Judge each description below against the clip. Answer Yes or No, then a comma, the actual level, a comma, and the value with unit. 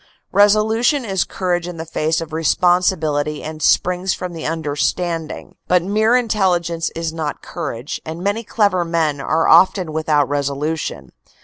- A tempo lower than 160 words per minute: Yes, average, 145 wpm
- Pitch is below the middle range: No, medium, 165 Hz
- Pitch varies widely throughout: No, average, 3.3 semitones